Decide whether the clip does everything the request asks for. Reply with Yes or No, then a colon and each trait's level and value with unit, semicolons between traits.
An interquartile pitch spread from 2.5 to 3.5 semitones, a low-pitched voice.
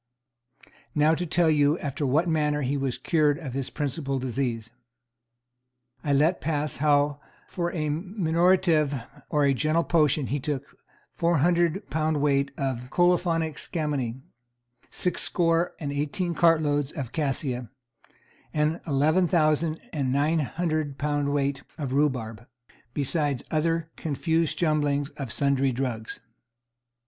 No: average, 2.9 semitones; medium, 150 Hz